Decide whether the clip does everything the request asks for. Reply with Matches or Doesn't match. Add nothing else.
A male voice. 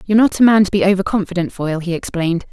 Doesn't match